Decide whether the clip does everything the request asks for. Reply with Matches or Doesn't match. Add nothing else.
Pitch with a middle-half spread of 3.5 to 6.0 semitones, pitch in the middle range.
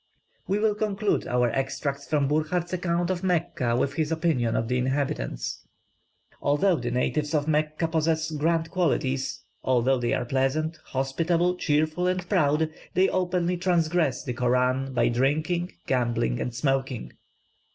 Matches